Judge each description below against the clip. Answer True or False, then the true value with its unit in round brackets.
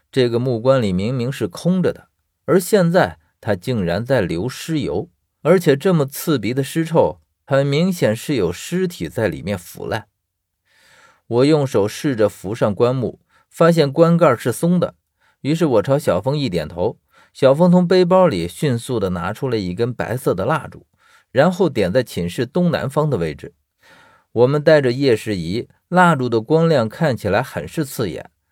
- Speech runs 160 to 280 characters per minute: True (245 characters per minute)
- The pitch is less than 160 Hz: True (135 Hz)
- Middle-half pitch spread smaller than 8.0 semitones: True (7.4 semitones)